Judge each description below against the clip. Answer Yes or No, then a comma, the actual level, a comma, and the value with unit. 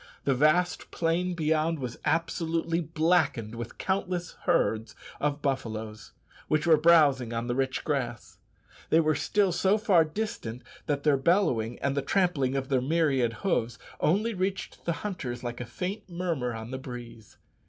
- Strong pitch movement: Yes, wide, 5.8 semitones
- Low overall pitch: No, medium, 150 Hz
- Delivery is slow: No, average, 155 wpm